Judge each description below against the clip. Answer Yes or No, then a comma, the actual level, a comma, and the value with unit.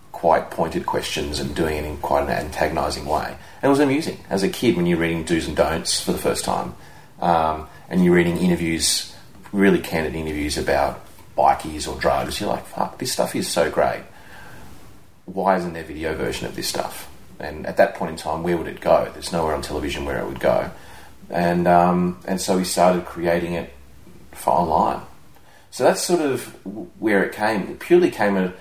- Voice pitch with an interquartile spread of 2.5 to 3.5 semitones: Yes, average, 2.9 semitones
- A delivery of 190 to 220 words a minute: Yes, fast, 205 wpm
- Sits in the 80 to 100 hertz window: Yes, very low, 85 Hz